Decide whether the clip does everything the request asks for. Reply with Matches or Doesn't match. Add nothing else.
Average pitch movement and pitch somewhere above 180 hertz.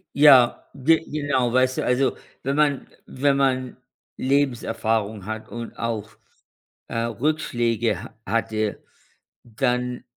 Doesn't match